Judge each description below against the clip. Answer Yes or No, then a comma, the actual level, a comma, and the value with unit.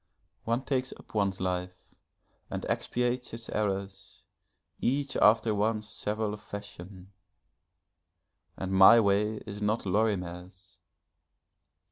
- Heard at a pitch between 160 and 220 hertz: No, low, 105 Hz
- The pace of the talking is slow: Yes, slow, 100 wpm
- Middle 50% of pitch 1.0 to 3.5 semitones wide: Yes, average, 2.8 semitones